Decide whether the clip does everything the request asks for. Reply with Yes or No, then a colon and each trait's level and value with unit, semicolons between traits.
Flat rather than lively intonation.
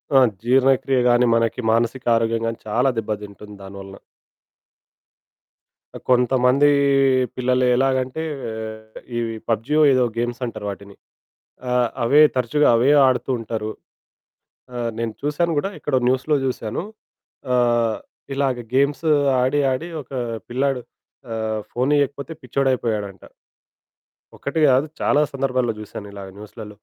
No: average, 3.2 semitones